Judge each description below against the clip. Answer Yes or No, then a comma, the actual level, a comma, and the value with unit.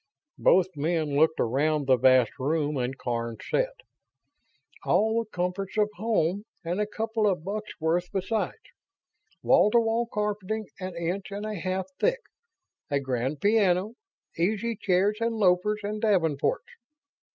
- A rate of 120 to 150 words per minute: Yes, average, 140 wpm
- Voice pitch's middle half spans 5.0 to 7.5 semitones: Yes, average, 5.3 semitones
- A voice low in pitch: No, medium, 185 Hz